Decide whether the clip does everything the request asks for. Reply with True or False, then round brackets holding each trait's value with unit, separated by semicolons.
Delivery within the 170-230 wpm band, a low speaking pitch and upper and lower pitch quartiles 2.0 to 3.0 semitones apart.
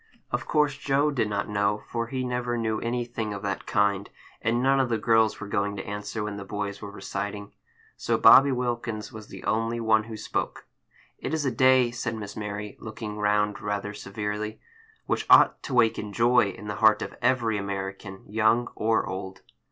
True (190 wpm; 110 Hz; 2.6 semitones)